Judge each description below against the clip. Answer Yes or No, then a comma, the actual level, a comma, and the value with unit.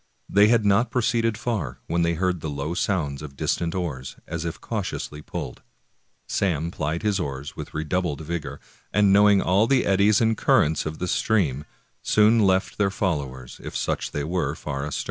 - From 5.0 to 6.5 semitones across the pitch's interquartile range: Yes, wide, 5.5 semitones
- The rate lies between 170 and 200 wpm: Yes, average, 185 wpm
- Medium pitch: No, very low, 85 Hz